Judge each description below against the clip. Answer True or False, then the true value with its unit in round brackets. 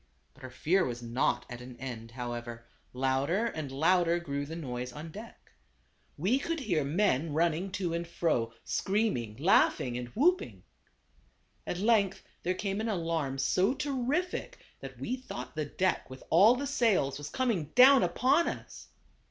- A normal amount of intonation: False (8.2 semitones)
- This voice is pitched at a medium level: True (170 Hz)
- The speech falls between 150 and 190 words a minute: True (160 wpm)